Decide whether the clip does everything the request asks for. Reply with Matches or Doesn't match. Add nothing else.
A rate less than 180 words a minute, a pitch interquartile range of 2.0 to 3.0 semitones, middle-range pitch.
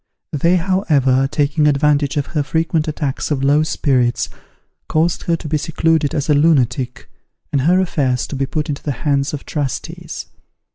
Matches